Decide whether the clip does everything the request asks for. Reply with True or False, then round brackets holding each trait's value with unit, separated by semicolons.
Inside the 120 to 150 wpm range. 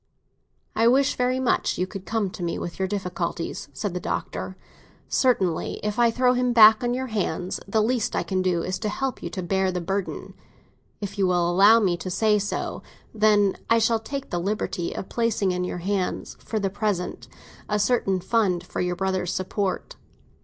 False (195 wpm)